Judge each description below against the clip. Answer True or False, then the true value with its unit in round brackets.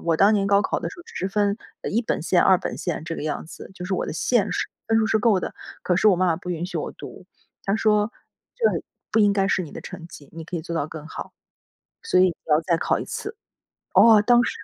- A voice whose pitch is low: False (190 Hz)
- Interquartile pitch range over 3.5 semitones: True (4.0 semitones)